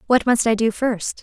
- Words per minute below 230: No, fast, 245 wpm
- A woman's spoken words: Yes, female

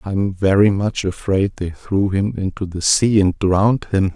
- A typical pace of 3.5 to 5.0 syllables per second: Yes, 4.5 syllables/s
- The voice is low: Yes, low, 100 Hz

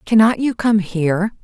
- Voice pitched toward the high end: Yes, high, 205 Hz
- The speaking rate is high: No, average, 165 wpm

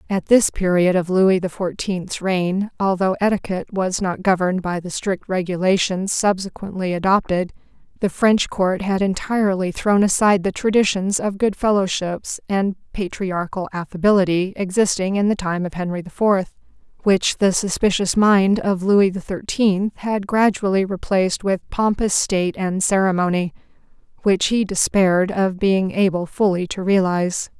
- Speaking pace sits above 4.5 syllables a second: Yes, 4.7 syllables/s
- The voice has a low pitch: No, high, 190 Hz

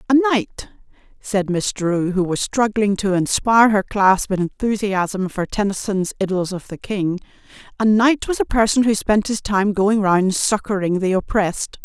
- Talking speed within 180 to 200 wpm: No, average, 170 wpm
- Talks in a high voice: Yes, high, 205 Hz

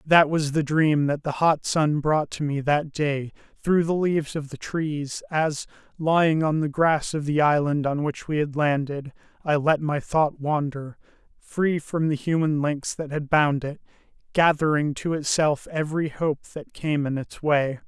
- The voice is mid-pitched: Yes, medium, 150 Hz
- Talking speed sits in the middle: Yes, average, 190 wpm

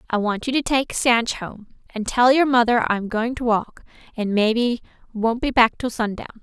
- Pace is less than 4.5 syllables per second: No, 4.7 syllables/s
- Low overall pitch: No, high, 235 Hz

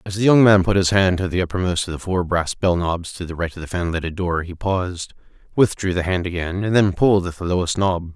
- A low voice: Yes, very low, 90 Hz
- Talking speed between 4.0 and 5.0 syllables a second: No, 5.9 syllables/s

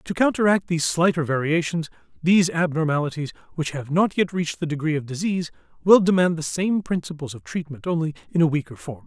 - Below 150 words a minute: No, average, 185 wpm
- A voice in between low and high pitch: Yes, medium, 165 Hz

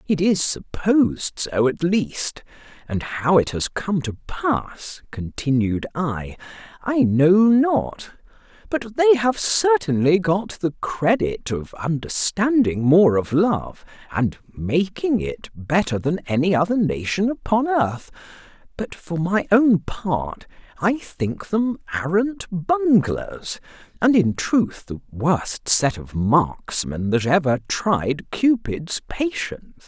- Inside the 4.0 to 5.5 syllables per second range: No, 3.4 syllables/s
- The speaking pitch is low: No, medium, 170 Hz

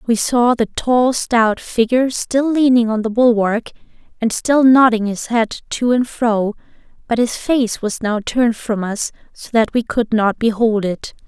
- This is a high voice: Yes, high, 230 Hz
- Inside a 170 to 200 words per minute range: Yes, average, 180 wpm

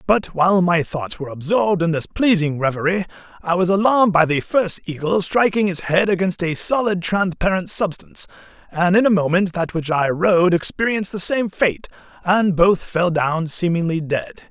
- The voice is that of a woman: No, male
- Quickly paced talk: No, average, 180 wpm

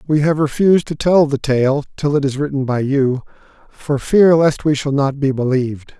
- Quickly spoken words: Yes, fast, 210 wpm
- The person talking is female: No, male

